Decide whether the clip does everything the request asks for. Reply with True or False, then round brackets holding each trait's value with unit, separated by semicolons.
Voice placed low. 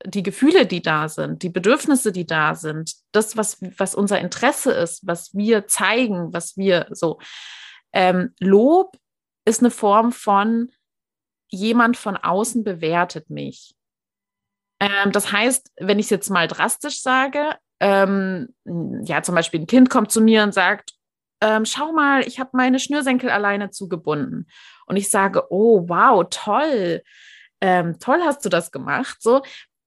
False (205 Hz)